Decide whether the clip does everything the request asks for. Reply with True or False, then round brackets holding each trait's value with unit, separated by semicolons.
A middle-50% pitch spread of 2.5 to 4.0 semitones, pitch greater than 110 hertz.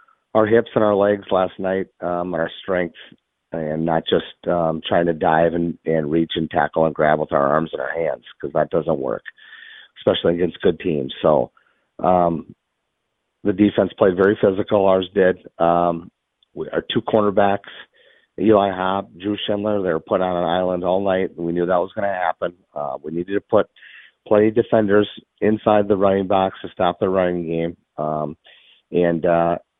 False (3.4 semitones; 90 Hz)